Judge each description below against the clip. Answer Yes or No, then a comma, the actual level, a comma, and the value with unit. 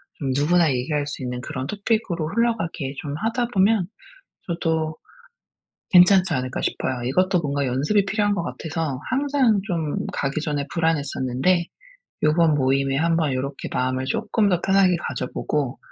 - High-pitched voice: No, medium, 160 Hz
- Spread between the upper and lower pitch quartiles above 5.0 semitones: Yes, wide, 5.4 semitones